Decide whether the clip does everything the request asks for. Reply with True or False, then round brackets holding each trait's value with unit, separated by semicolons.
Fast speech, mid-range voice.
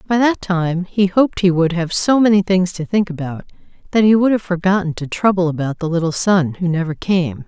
True (225 wpm; 180 Hz)